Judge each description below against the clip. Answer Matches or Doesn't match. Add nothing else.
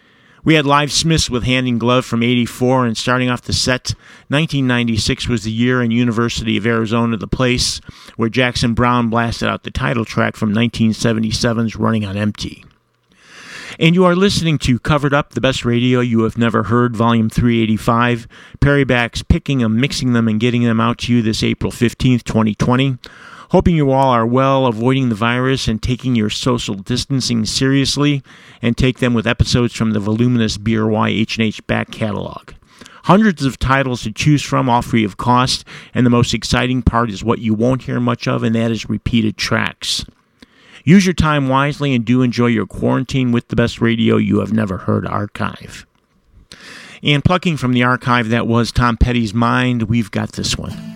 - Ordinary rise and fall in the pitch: Doesn't match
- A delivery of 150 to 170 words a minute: Doesn't match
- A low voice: Matches